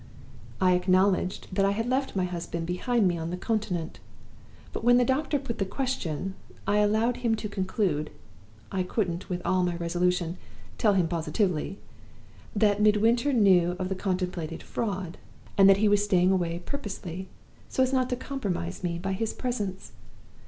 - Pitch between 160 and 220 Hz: Yes, high, 190 Hz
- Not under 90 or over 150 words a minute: No, average, 165 wpm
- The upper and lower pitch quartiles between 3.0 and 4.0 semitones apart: Yes, average, 3.7 semitones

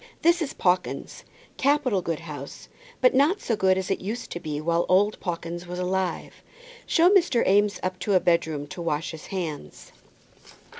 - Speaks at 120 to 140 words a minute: No, average, 170 wpm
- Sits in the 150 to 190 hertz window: Yes, medium, 185 Hz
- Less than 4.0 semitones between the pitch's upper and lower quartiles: No, average, 4.6 semitones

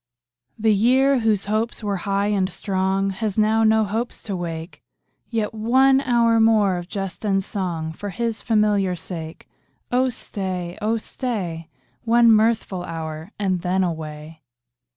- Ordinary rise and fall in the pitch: Yes, average, 3.7 semitones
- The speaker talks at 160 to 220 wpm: No, average, 145 wpm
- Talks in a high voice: Yes, high, 205 Hz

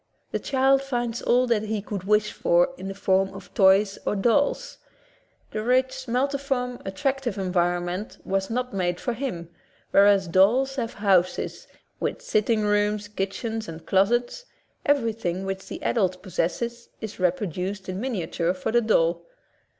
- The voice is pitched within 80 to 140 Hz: No, high, 210 Hz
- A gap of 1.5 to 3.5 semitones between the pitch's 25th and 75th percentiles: No, average, 4.3 semitones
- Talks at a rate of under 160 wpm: Yes, average, 150 wpm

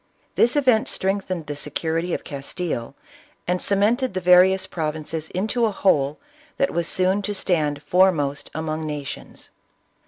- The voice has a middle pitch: Yes, medium, 180 Hz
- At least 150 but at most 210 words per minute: No, slow, 135 wpm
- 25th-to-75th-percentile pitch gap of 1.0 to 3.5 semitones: No, average, 4.1 semitones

